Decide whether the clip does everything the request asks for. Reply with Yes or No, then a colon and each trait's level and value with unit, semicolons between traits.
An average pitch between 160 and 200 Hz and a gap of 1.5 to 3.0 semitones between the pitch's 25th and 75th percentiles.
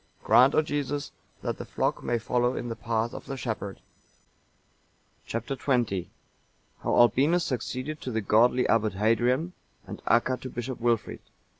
No: low, 120 Hz; narrow, 2.6 semitones